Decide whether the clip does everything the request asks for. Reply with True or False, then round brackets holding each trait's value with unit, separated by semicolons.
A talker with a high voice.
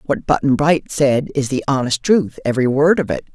False (140 Hz)